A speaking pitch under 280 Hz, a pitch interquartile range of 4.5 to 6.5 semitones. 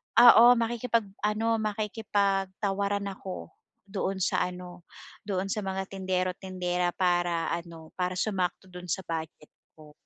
No: high, 190 Hz; narrow, 2.4 semitones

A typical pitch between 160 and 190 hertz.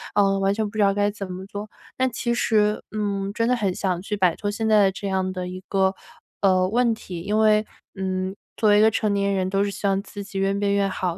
No: high, 200 Hz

